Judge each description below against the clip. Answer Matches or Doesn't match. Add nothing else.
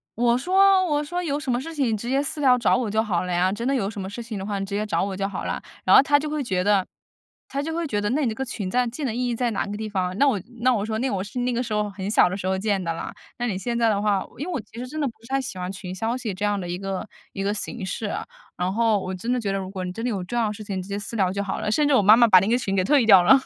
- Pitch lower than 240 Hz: Matches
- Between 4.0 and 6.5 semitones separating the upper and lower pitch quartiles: Matches